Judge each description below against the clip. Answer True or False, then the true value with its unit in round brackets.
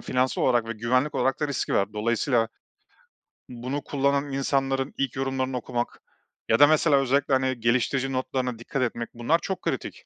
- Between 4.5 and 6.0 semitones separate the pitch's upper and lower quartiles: False (2.4 semitones)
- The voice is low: True (130 Hz)